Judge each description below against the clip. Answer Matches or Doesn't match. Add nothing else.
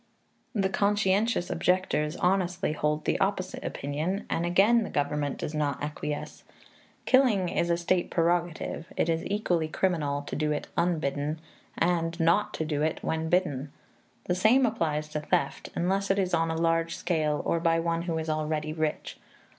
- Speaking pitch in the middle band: Matches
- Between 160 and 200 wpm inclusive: Matches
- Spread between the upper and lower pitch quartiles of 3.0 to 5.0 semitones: Matches